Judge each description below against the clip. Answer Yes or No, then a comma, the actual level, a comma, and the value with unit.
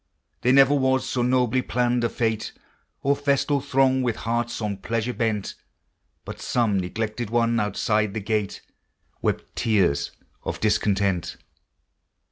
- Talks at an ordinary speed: No, slow, 130 wpm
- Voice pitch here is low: Yes, low, 115 Hz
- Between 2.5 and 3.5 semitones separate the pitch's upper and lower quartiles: Yes, average, 3.1 semitones